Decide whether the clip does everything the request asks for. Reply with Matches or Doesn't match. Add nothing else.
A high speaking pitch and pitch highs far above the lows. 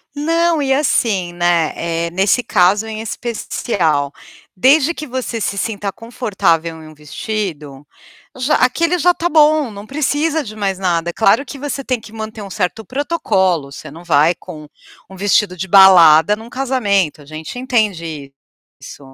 Matches